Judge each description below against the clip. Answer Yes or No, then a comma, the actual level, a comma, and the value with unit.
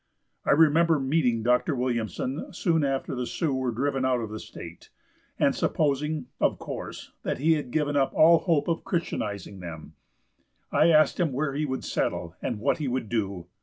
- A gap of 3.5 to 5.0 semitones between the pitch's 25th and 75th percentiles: Yes, average, 4.4 semitones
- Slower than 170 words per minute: No, average, 180 wpm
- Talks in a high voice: No, low, 135 Hz